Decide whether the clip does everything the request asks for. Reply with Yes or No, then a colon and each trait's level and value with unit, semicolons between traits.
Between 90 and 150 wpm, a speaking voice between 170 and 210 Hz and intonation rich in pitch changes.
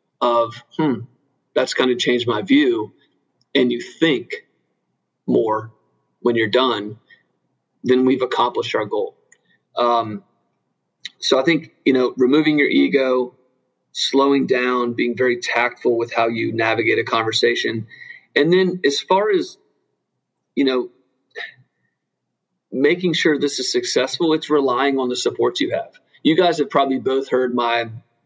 No: average, 145 wpm; low, 130 Hz; wide, 6.1 semitones